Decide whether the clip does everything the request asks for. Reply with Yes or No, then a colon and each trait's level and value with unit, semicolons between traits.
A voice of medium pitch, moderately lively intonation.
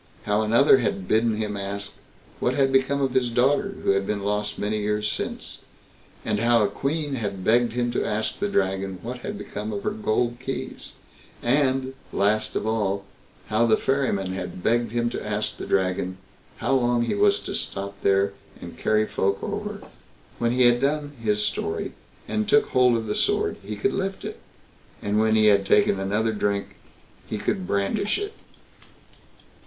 No: low, 110 Hz; average, 3.9 semitones